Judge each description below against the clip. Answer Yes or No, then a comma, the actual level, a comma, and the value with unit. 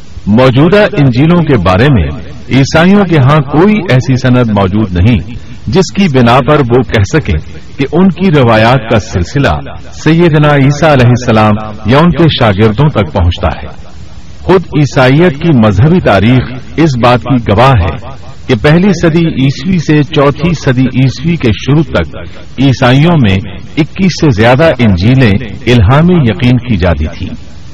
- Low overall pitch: Yes, low, 130 Hz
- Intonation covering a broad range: Yes, wide, 6.2 semitones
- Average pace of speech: Yes, average, 150 wpm